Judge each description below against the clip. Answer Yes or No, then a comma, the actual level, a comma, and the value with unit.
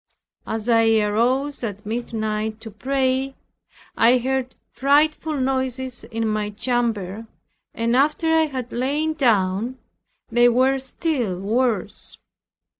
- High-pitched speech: Yes, high, 245 Hz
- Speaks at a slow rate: Yes, slow, 115 wpm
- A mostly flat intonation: No, average, 3.4 semitones